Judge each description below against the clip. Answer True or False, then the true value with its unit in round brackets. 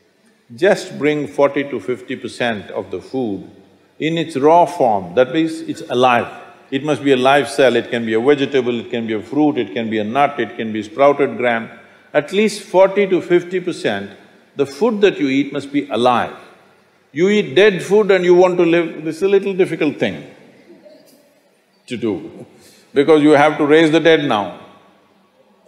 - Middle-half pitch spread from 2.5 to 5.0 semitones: False (5.5 semitones)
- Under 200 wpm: True (190 wpm)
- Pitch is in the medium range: True (150 Hz)